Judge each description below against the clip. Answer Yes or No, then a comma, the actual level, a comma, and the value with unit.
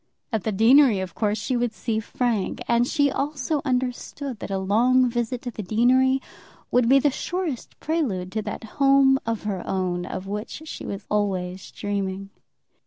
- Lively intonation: No, average, 4.6 semitones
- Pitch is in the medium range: No, high, 230 Hz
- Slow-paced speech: No, average, 175 wpm